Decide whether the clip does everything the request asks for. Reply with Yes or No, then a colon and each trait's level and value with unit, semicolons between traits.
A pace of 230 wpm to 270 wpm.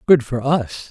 No: average, 200 wpm